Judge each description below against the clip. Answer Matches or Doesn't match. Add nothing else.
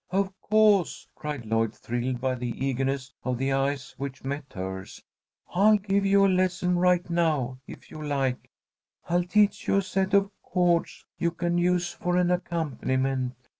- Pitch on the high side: Doesn't match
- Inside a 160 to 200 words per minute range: Matches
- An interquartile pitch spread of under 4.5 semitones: Doesn't match